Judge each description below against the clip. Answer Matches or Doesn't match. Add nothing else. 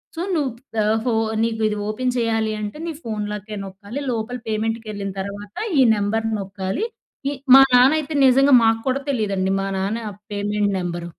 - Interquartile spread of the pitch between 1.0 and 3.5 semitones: Matches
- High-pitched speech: Matches